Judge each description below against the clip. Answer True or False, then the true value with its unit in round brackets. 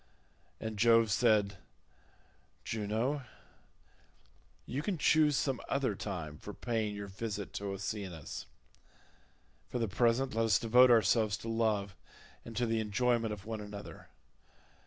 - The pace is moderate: False (125 wpm)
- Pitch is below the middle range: True (110 Hz)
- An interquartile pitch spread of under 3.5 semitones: True (2.7 semitones)